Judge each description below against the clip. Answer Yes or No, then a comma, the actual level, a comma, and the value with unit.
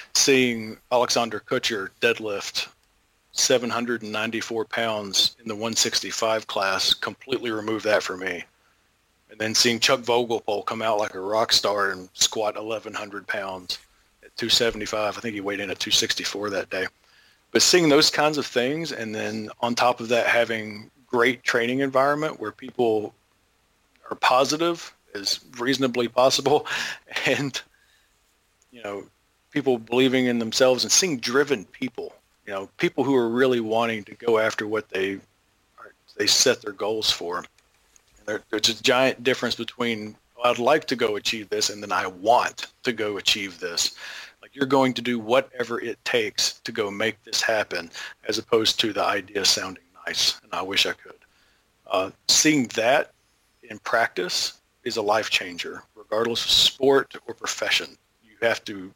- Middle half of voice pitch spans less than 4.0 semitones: Yes, average, 3.6 semitones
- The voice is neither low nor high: No, low, 120 Hz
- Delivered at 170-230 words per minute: No, average, 155 wpm